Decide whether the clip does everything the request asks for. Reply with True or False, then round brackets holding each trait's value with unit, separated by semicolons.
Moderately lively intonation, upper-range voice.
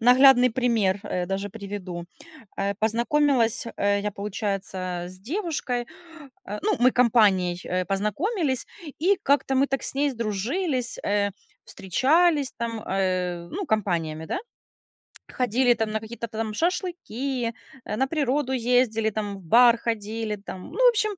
True (4.7 semitones; 230 Hz)